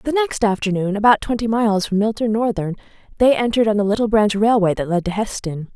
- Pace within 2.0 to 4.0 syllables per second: No, 6.4 syllables/s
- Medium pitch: No, high, 205 Hz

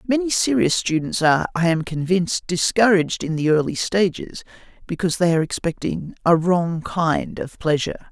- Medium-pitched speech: Yes, medium, 170 Hz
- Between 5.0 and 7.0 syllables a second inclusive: Yes, 5.3 syllables/s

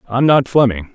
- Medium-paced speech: Yes, average, 190 wpm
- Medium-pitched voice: No, low, 120 Hz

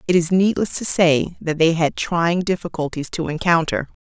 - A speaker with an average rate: Yes, average, 180 wpm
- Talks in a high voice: No, medium, 170 Hz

